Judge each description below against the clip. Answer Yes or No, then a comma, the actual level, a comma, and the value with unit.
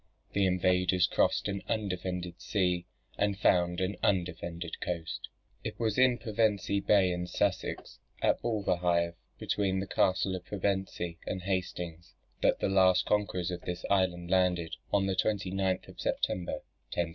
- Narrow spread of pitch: Yes, narrow, 2.1 semitones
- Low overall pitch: Yes, very low, 95 Hz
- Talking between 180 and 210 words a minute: No, average, 145 wpm